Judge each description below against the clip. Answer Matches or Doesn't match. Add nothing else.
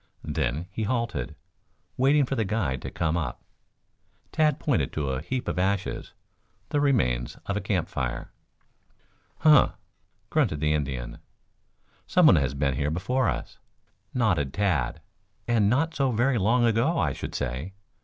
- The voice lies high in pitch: Doesn't match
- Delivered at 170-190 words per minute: Doesn't match